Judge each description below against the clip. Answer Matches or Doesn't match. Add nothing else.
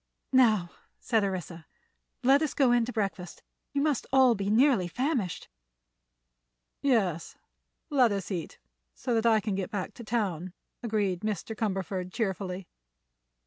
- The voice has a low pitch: Doesn't match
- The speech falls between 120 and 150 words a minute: Matches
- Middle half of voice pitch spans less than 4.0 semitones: Doesn't match